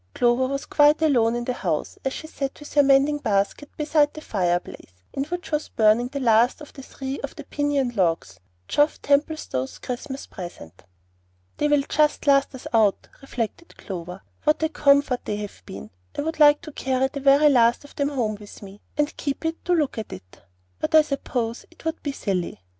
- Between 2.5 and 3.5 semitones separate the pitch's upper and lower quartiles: No, average, 4.9 semitones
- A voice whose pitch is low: No, very high, 270 Hz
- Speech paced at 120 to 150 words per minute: No, average, 190 wpm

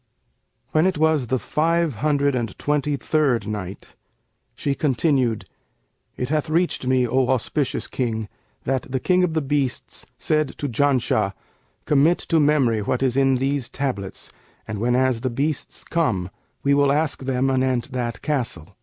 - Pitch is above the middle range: No, low, 135 Hz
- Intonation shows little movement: No, average, 3.3 semitones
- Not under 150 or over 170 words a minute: Yes, average, 155 wpm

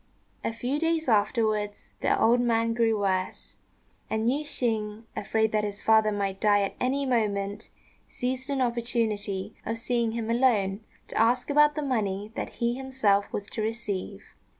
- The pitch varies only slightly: No, average, 3.1 semitones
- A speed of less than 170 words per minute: Yes, average, 160 wpm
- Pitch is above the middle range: Yes, high, 225 Hz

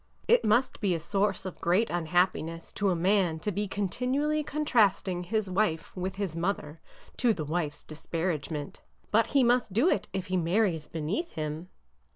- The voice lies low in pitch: No, medium, 185 Hz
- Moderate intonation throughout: Yes, average, 4.5 semitones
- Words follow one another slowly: No, average, 170 wpm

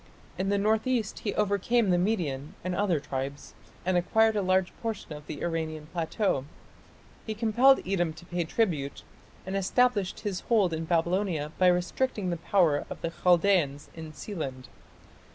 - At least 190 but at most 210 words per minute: No, average, 160 wpm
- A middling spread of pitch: Yes, average, 4.3 semitones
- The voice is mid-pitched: Yes, medium, 180 Hz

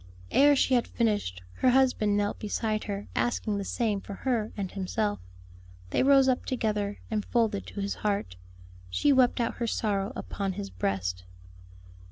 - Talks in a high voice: Yes, high, 210 Hz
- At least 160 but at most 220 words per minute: Yes, average, 165 wpm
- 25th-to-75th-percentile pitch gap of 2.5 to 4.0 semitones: Yes, average, 3.3 semitones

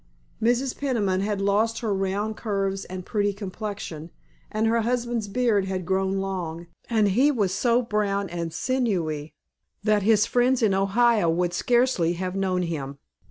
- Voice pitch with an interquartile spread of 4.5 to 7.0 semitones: No, average, 3.5 semitones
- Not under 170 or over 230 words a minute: No, average, 155 wpm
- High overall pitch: Yes, high, 200 Hz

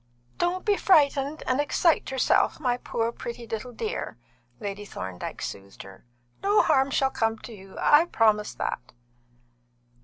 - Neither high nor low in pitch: No, very high, 250 Hz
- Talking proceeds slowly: No, average, 145 wpm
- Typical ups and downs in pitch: No, wide, 5.9 semitones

